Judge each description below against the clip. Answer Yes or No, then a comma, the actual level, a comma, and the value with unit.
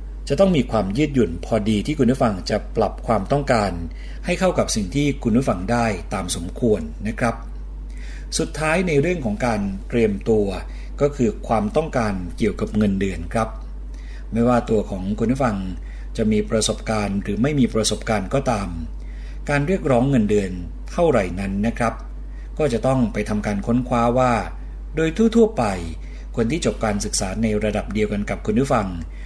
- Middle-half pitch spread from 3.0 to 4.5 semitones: No, average, 5.2 semitones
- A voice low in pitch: Yes, low, 105 Hz